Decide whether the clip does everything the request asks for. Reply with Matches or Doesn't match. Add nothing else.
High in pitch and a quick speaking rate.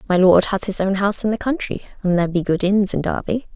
Matches